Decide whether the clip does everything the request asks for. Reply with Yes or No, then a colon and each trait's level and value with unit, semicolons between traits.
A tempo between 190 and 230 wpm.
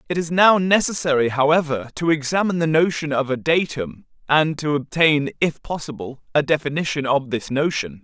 No: average, 165 wpm